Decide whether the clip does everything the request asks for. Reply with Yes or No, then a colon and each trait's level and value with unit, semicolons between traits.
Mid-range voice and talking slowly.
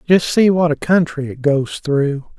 No: medium, 155 Hz; average, 200 wpm